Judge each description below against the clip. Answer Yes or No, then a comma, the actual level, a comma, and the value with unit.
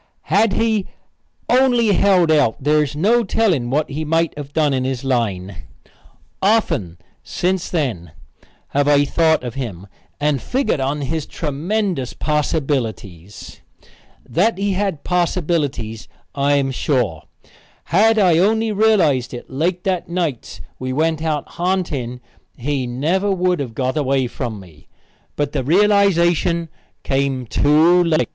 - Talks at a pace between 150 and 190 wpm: No, slow, 135 wpm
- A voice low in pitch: No, medium, 150 Hz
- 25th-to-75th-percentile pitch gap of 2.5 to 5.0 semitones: No, wide, 5.6 semitones